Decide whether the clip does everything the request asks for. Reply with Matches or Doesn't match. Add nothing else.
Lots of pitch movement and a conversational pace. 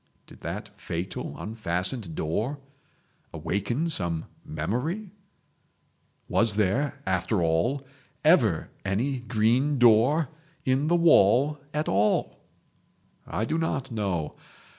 Doesn't match